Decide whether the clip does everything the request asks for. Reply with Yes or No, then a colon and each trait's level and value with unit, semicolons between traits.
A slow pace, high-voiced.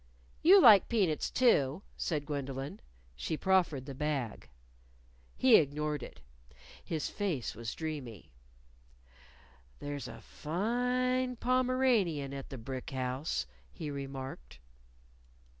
No: slow, 105 wpm; medium, 150 Hz